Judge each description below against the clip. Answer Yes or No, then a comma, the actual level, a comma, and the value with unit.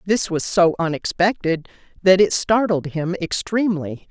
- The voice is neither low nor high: Yes, medium, 180 Hz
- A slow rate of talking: Yes, slow, 130 wpm